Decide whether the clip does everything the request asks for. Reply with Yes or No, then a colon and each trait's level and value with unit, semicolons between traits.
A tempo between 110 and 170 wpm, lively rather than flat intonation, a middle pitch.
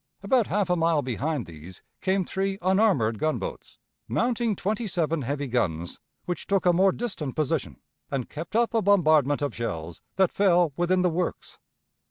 Yes: average, 165 wpm; wide, 6.2 semitones; medium, 170 Hz